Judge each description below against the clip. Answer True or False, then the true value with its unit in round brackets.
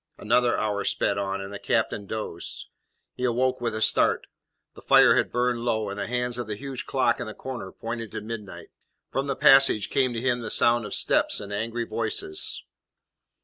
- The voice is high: False (115 Hz)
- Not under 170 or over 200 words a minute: True (195 wpm)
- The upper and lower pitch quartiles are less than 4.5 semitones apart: True (2.8 semitones)